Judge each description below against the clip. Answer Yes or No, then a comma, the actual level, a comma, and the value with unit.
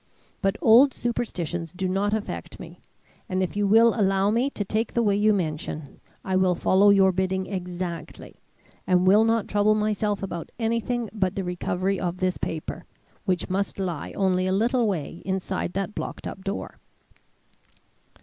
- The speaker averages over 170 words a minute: No, average, 165 wpm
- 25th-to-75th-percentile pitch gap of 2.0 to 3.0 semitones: Yes, narrow, 2.5 semitones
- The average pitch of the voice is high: Yes, high, 195 Hz